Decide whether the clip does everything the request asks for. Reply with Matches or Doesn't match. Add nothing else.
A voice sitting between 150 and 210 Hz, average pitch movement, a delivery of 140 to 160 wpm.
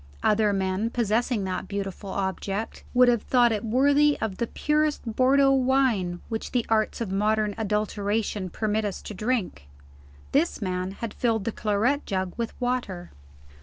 Doesn't match